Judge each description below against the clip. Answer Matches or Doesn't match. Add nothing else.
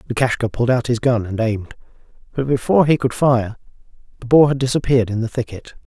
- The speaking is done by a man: Matches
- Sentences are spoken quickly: Doesn't match